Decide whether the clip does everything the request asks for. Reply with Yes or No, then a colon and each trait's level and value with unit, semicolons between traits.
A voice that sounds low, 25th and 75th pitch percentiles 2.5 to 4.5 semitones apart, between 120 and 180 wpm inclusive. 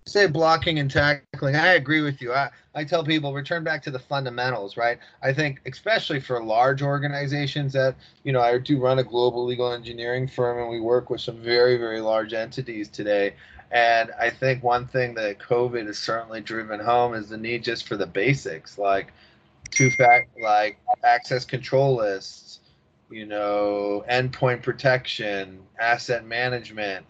Yes: low, 125 Hz; average, 3.5 semitones; average, 170 wpm